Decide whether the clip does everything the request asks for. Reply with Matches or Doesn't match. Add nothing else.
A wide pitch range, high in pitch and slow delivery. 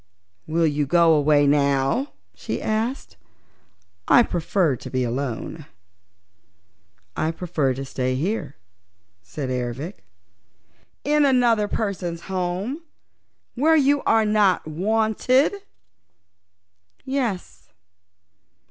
Doesn't match